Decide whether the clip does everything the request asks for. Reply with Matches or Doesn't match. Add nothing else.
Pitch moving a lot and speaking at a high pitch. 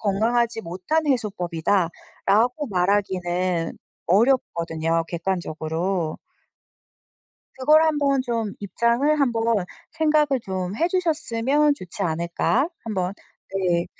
Matches